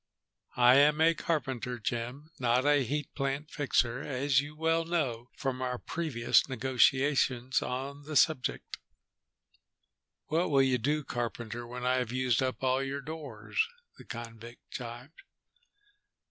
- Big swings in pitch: No, average, 3.1 semitones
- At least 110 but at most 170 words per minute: Yes, slow, 135 wpm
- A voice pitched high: No, low, 130 Hz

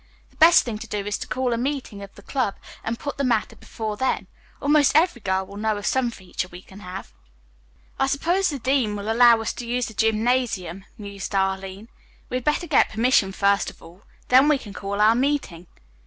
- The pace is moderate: No, fast, 215 wpm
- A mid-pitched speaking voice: No, high, 225 Hz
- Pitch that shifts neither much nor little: Yes, average, 4.6 semitones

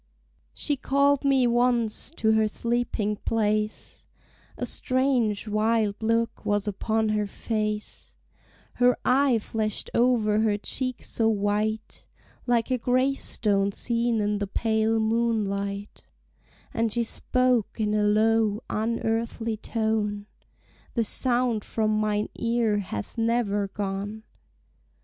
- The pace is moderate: No, slow, 115 wpm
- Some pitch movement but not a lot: No, narrow, 2.0 semitones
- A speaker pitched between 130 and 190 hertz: No, high, 220 Hz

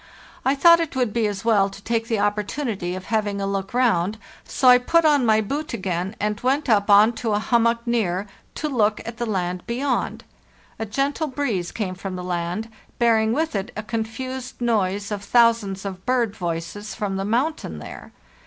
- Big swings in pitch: No, average, 3.9 semitones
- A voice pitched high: Yes, high, 220 Hz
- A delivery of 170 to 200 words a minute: Yes, average, 190 wpm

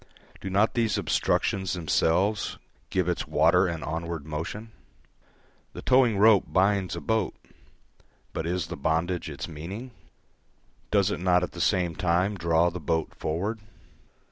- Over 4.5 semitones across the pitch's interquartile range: No, average, 3.4 semitones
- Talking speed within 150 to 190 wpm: No, average, 140 wpm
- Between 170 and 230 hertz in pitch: No, very low, 90 Hz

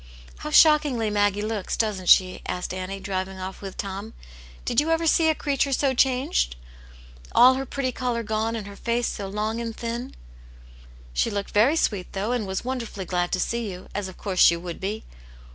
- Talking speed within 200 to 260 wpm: Yes, fast, 205 wpm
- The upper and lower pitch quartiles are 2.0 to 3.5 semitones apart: No, average, 4.6 semitones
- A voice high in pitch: Yes, high, 210 Hz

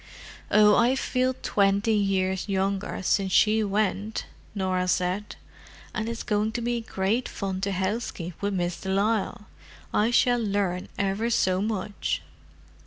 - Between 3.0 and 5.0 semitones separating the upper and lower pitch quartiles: No, narrow, 2.5 semitones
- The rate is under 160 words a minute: Yes, average, 140 wpm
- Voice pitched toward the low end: No, high, 200 Hz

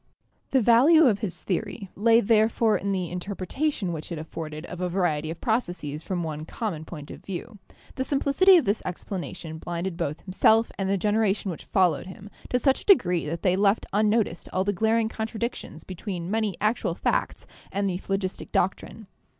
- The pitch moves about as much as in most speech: Yes, average, 4.2 semitones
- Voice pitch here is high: Yes, high, 195 Hz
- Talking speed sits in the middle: Yes, average, 185 wpm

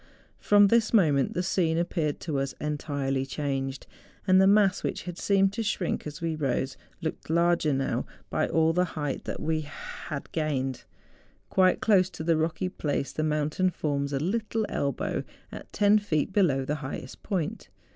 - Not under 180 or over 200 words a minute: No, average, 165 wpm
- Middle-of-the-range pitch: Yes, medium, 160 Hz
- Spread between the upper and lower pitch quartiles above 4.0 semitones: Yes, average, 4.6 semitones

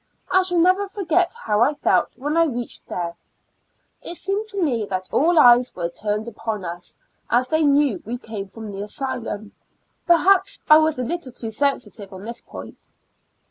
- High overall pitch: Yes, very high, 250 Hz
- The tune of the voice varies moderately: No, wide, 7.9 semitones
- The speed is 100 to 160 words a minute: No, average, 180 wpm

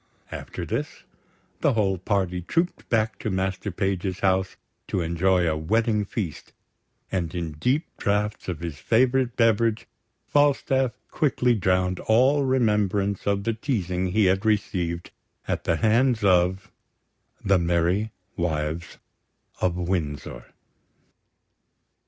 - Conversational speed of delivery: No, slow, 120 wpm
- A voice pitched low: Yes, very low, 95 Hz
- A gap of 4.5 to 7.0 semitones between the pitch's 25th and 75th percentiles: No, average, 4.1 semitones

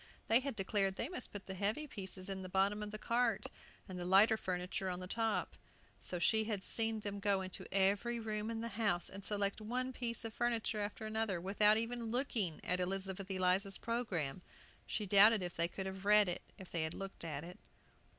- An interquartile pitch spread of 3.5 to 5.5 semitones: No, average, 2.9 semitones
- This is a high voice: Yes, high, 200 Hz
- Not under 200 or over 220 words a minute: Yes, fast, 205 wpm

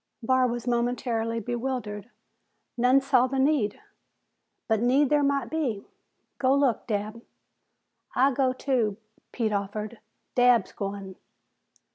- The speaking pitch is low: No, high, 245 Hz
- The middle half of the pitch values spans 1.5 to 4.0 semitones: Yes, average, 3.4 semitones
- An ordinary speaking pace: No, slow, 115 wpm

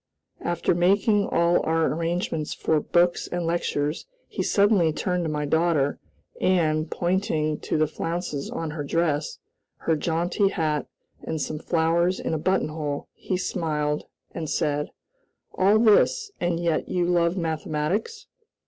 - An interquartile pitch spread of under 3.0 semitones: Yes, narrow, 2.5 semitones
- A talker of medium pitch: Yes, medium, 165 Hz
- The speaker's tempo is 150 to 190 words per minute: No, average, 140 wpm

